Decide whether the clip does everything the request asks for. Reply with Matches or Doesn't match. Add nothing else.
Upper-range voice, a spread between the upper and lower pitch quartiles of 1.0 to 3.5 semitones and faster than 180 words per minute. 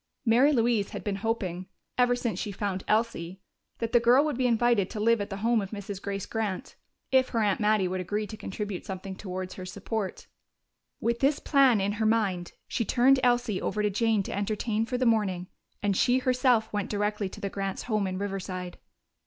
Matches